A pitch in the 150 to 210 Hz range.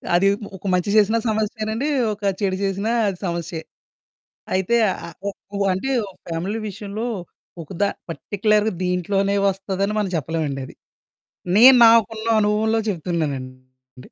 Yes: high, 195 Hz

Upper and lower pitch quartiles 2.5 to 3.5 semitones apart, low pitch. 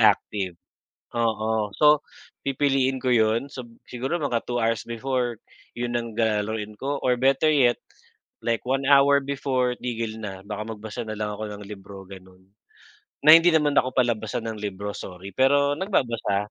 No: average, 4.0 semitones; low, 115 Hz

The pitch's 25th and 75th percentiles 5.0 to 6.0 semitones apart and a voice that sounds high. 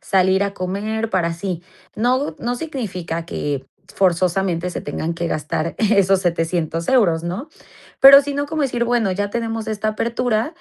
Yes: wide, 5.4 semitones; high, 195 Hz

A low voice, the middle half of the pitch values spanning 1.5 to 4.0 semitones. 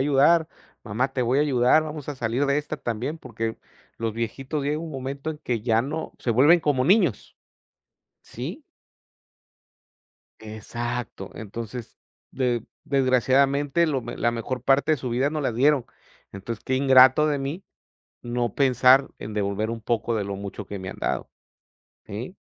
Yes: low, 130 Hz; average, 3.7 semitones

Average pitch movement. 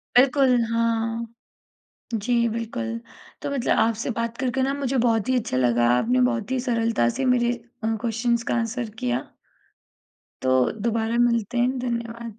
No: narrow, 1.9 semitones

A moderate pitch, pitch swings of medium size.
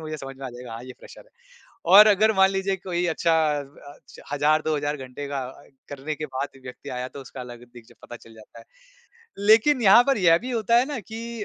No: medium, 155 Hz; wide, 7.7 semitones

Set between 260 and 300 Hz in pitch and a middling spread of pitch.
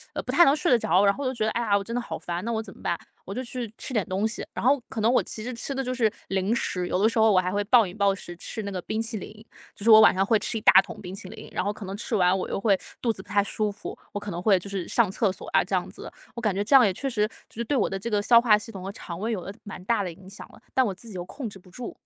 No: high, 210 Hz; average, 3.2 semitones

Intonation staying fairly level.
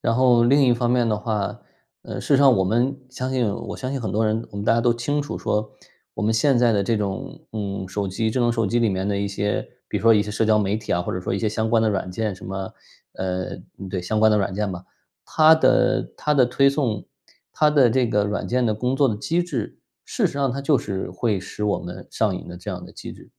No: average, 3.7 semitones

